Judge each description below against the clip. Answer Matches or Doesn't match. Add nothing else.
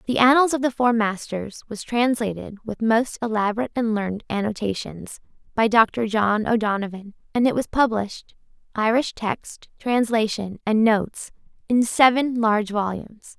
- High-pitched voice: Matches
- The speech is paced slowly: Matches